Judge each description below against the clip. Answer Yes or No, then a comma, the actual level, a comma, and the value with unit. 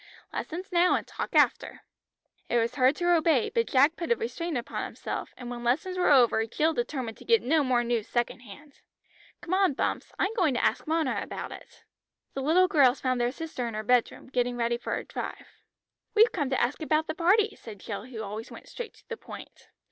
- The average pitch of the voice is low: No, very high, 275 Hz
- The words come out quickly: Yes, fast, 215 wpm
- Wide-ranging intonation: Yes, wide, 6.1 semitones